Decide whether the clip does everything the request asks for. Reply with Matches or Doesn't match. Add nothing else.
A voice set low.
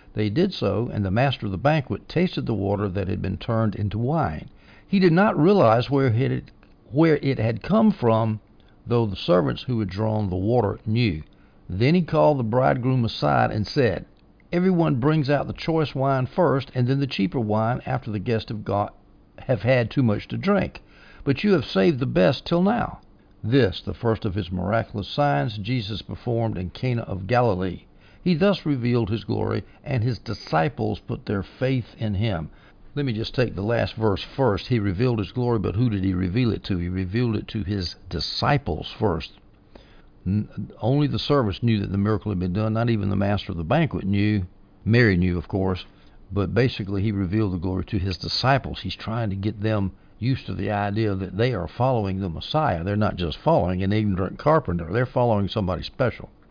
Matches